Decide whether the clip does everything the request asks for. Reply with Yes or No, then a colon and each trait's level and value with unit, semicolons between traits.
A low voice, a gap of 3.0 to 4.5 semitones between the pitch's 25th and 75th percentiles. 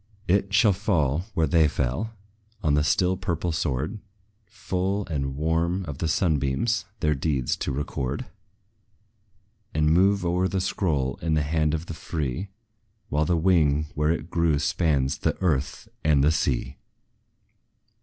Yes: very low, 80 Hz; average, 4.0 semitones